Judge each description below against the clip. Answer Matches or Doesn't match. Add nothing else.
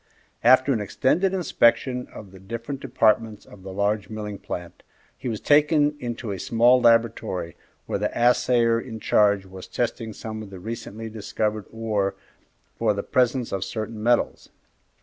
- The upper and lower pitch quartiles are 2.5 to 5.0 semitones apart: Matches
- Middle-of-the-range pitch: Doesn't match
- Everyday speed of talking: Matches